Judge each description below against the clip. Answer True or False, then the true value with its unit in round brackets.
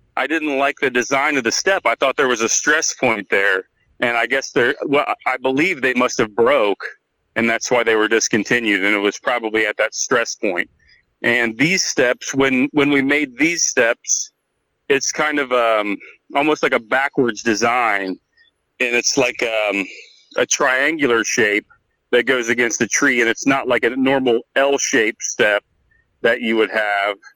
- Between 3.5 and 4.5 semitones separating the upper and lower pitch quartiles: True (3.9 semitones)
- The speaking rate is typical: True (185 wpm)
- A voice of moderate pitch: False (130 Hz)